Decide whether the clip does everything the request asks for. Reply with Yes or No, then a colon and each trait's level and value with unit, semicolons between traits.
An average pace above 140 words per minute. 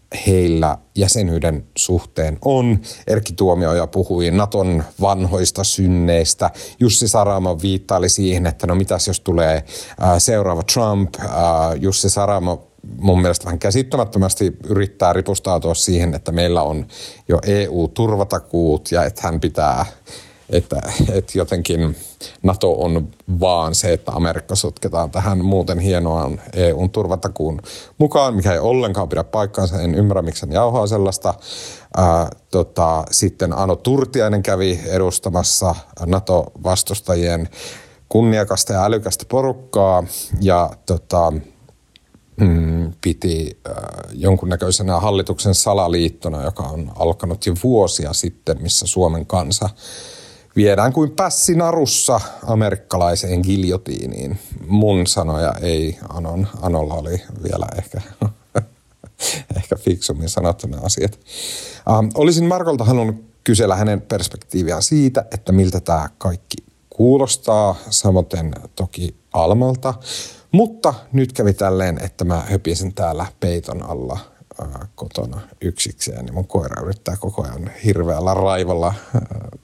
No: average, 110 wpm